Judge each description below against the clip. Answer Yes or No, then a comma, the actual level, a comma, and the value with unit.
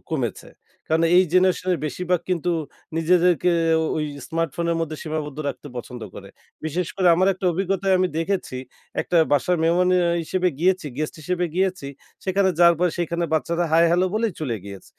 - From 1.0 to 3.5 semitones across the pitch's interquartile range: Yes, narrow, 2.5 semitones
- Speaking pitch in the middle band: Yes, medium, 175 Hz